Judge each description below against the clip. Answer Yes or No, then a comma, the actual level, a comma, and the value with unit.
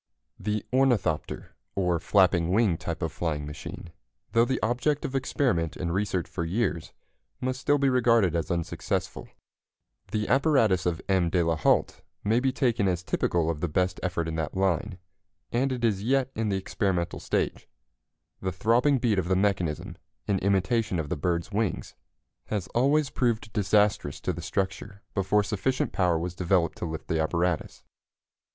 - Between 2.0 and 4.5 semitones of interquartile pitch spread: No, average, 5.2 semitones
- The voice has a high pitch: No, very low, 95 Hz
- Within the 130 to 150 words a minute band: No, average, 165 wpm